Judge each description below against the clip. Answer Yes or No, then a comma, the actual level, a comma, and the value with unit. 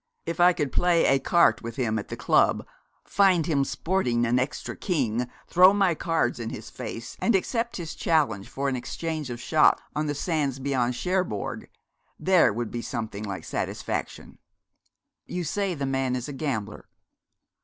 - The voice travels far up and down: Yes, wide, 6.2 semitones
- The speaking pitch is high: No, medium, 140 Hz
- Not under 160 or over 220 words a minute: Yes, average, 165 wpm